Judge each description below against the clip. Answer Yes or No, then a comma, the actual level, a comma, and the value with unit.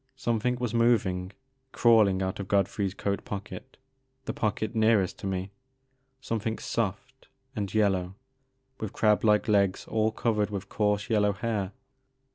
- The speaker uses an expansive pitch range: No, average, 2.8 semitones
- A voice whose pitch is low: Yes, low, 105 Hz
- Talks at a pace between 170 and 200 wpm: No, average, 155 wpm